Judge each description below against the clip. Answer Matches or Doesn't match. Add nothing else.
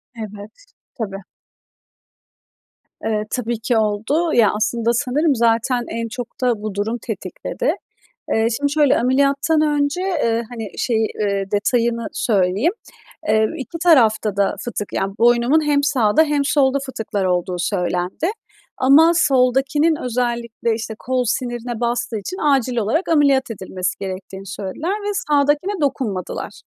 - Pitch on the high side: Matches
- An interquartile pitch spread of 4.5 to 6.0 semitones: Matches